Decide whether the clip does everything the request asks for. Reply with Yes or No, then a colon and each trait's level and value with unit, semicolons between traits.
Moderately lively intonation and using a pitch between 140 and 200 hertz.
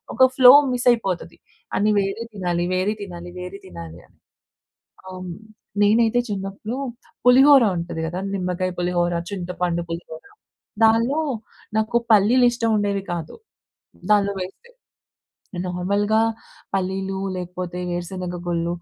Yes: average, 3.4 semitones; high, 190 Hz